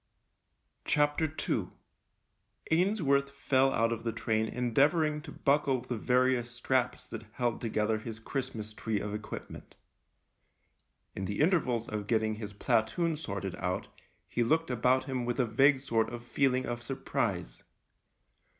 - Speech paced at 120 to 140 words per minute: Yes, slow, 135 wpm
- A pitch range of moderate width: Yes, average, 3.9 semitones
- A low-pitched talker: Yes, low, 120 Hz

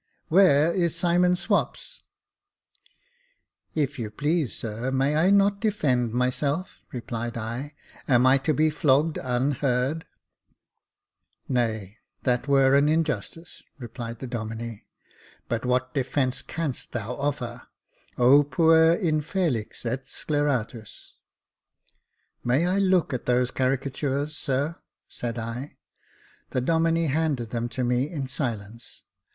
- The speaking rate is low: Yes, slow, 125 wpm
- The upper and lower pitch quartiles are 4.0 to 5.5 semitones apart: Yes, average, 4.4 semitones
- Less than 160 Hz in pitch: Yes, low, 135 Hz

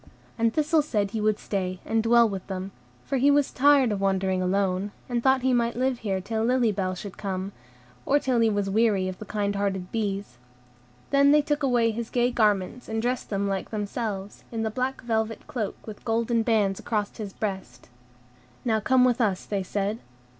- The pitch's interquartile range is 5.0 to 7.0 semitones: No, average, 3.6 semitones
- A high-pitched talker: Yes, high, 220 Hz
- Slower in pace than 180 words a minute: No, average, 195 wpm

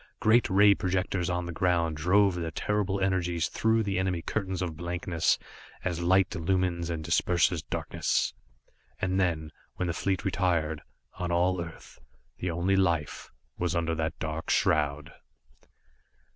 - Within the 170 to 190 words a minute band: No, average, 145 wpm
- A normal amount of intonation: No, narrow, 2.2 semitones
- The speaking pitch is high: No, very low, 90 Hz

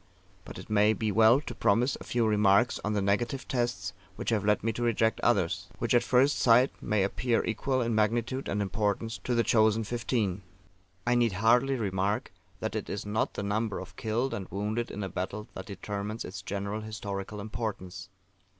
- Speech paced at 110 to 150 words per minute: No, average, 190 wpm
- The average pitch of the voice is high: No, low, 110 Hz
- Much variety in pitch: No, average, 2.8 semitones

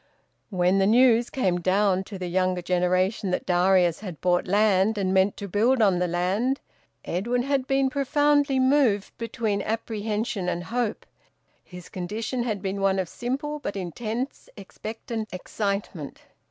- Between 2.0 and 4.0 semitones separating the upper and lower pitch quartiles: No, average, 4.4 semitones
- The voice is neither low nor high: No, high, 205 Hz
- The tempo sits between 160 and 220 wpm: No, average, 150 wpm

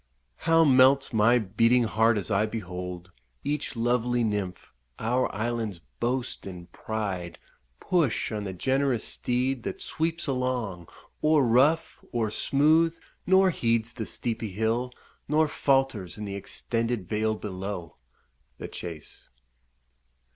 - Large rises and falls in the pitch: No, average, 4.4 semitones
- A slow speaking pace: Yes, slow, 125 wpm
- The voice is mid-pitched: No, low, 115 Hz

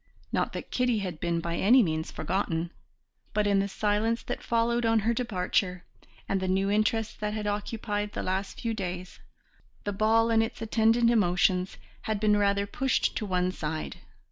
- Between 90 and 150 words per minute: No, average, 175 wpm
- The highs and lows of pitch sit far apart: No, average, 3.4 semitones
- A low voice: No, high, 205 Hz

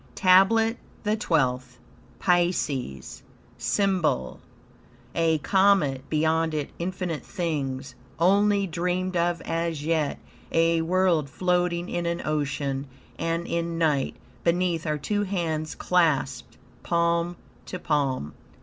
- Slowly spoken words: Yes, slow, 105 wpm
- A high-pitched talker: No, medium, 170 Hz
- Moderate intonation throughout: Yes, average, 3.2 semitones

